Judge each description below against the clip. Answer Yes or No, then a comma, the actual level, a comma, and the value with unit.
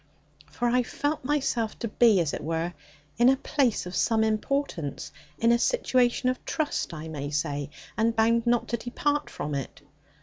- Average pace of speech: Yes, average, 175 wpm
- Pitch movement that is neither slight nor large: No, wide, 7.3 semitones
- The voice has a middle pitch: No, high, 230 Hz